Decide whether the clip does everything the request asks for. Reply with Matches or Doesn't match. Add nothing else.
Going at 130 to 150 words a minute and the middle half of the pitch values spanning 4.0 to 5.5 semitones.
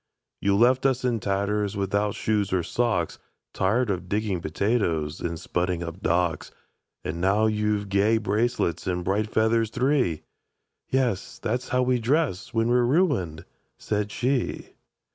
Matches